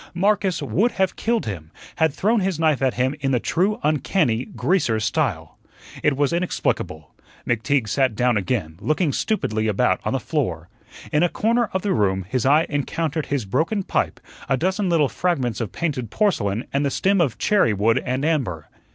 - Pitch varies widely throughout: Yes, wide, 7.7 semitones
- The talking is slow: No, average, 180 wpm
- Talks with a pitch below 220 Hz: Yes, medium, 140 Hz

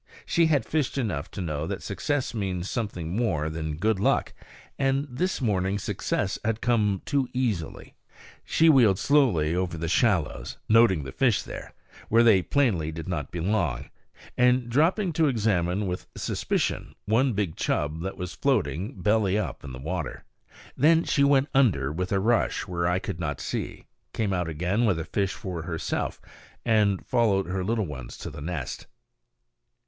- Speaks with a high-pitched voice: No, low, 100 Hz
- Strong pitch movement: Yes, wide, 6.2 semitones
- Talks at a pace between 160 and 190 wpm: Yes, average, 165 wpm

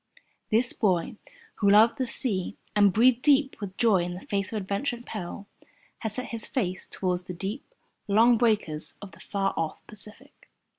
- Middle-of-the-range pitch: No, high, 210 Hz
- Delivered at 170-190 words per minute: Yes, average, 180 wpm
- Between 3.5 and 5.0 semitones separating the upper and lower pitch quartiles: Yes, average, 3.9 semitones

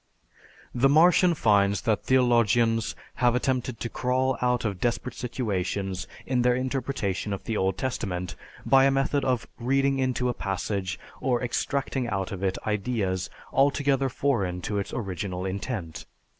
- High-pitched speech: No, low, 120 Hz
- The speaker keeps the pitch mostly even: No, average, 4.9 semitones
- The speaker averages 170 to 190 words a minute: No, average, 145 wpm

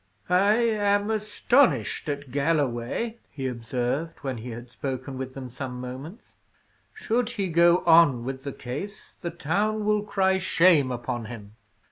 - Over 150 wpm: No, average, 145 wpm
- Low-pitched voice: No, medium, 150 Hz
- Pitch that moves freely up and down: Yes, wide, 8.1 semitones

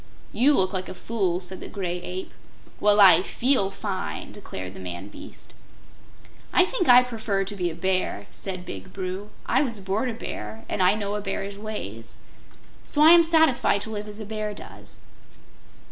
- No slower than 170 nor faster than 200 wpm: Yes, average, 185 wpm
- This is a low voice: No, high, 200 Hz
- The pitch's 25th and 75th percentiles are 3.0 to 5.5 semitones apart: Yes, average, 3.3 semitones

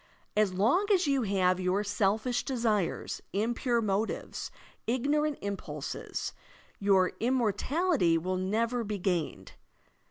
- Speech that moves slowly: Yes, slow, 105 wpm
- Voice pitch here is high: Yes, high, 215 Hz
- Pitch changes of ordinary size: Yes, average, 4.4 semitones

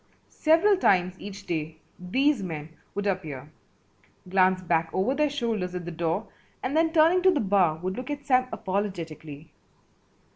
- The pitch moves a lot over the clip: Yes, wide, 7.7 semitones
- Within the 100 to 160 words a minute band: Yes, average, 155 wpm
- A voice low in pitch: No, high, 190 Hz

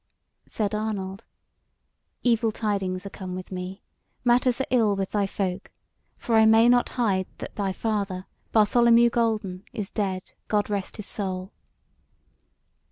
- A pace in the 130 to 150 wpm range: Yes, average, 140 wpm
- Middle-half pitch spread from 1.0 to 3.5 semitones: Yes, average, 3.0 semitones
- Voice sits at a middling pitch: No, high, 205 Hz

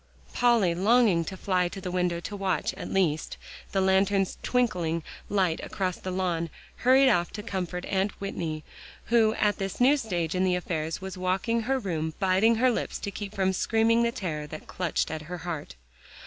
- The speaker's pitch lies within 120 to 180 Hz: No, high, 190 Hz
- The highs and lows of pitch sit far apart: No, average, 3.8 semitones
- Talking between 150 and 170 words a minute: No, average, 185 wpm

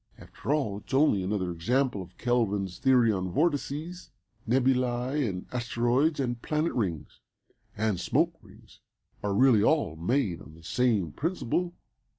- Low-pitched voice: Yes, low, 120 Hz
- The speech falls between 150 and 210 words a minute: No, average, 140 wpm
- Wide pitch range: Yes, wide, 5.7 semitones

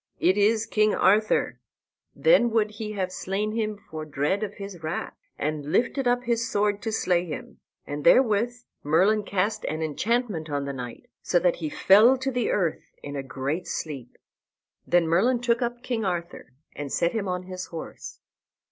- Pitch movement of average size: No, wide, 6.1 semitones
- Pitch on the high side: Yes, high, 200 Hz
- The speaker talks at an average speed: Yes, average, 175 wpm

